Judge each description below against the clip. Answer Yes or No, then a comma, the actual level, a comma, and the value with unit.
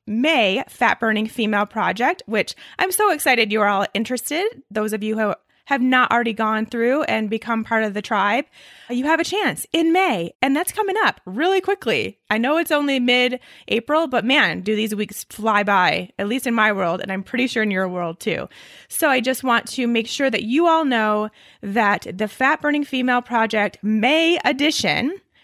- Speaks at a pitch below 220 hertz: No, high, 235 Hz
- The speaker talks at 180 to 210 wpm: Yes, average, 200 wpm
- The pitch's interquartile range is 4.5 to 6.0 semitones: Yes, wide, 5.4 semitones